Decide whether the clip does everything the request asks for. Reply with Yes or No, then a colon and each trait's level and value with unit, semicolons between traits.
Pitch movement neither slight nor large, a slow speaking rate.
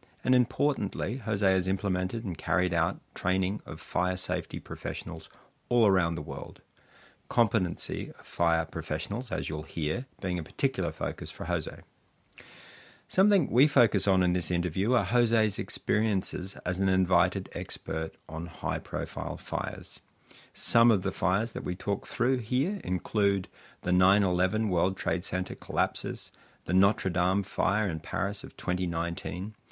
No: average, 3.9 semitones; average, 145 wpm